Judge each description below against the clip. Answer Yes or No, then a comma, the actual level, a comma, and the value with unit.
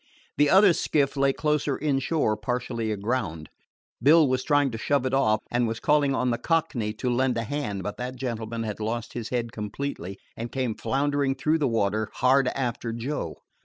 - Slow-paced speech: No, average, 185 wpm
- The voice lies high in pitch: No, low, 125 Hz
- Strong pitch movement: No, average, 3.8 semitones